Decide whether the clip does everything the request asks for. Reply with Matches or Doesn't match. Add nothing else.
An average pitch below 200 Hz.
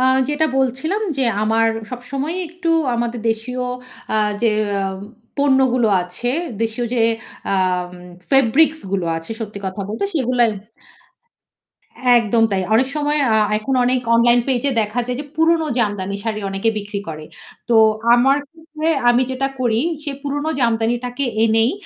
Doesn't match